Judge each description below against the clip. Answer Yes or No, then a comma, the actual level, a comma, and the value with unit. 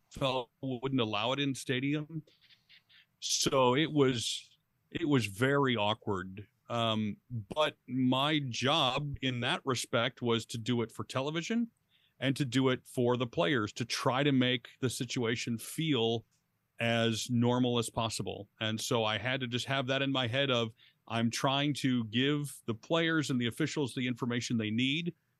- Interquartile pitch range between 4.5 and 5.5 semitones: No, average, 3.0 semitones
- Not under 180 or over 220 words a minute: No, average, 165 wpm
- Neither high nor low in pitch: No, low, 130 Hz